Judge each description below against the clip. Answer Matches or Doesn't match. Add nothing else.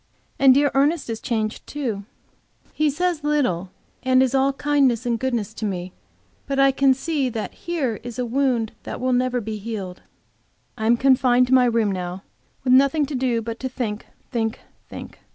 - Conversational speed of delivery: Matches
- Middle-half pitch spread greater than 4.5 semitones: Doesn't match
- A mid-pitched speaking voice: Doesn't match